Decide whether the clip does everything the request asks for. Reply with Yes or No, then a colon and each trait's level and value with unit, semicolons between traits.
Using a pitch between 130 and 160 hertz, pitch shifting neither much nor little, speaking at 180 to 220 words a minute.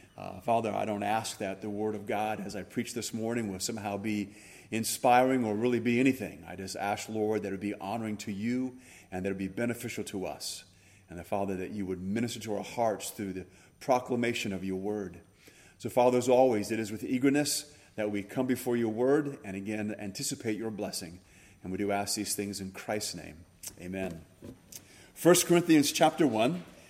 No: low, 105 Hz; average, 3.6 semitones; average, 200 wpm